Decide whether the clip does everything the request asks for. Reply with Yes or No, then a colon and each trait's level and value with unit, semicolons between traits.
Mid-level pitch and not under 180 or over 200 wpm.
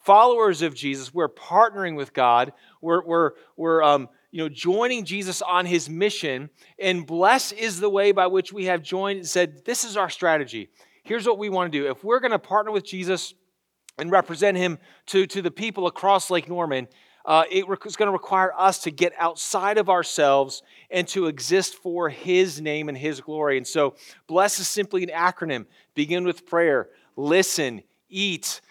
Yes: medium, 180 Hz; average, 185 wpm